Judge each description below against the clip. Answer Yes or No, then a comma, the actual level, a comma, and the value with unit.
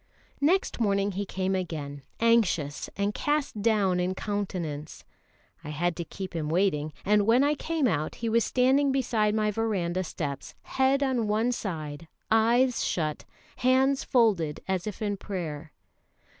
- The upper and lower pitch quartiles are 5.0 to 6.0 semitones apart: Yes, wide, 5.4 semitones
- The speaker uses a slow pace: No, average, 150 wpm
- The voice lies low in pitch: No, high, 205 Hz